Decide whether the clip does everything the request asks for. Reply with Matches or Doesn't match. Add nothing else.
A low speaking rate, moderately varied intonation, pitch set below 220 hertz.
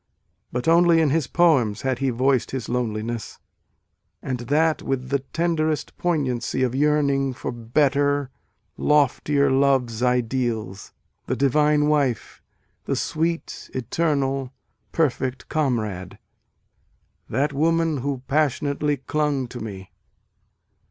Matches